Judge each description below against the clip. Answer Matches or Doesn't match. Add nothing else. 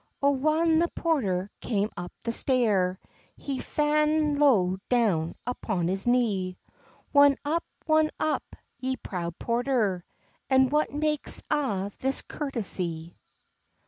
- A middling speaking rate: Doesn't match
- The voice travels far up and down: Matches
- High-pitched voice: Matches